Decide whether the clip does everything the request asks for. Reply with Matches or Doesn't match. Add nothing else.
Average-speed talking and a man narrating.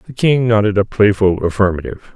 Matches